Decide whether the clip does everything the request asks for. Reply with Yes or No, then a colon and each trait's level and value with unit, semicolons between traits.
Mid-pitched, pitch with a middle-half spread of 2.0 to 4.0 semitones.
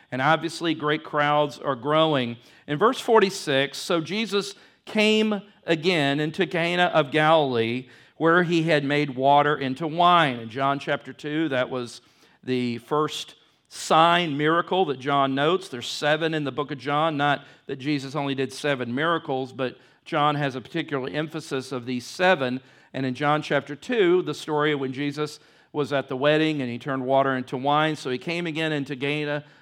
Yes: medium, 150 Hz; average, 3.1 semitones